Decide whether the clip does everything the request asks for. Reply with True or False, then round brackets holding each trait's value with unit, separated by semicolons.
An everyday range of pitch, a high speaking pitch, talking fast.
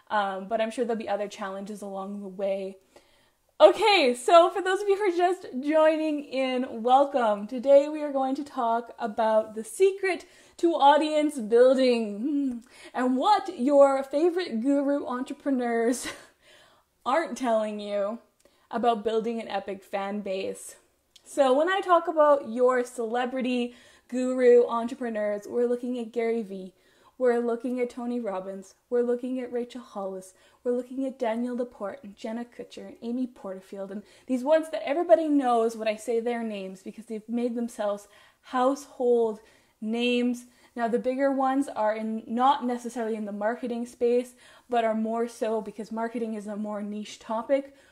False (3.7 semitones; 240 Hz; 155 wpm)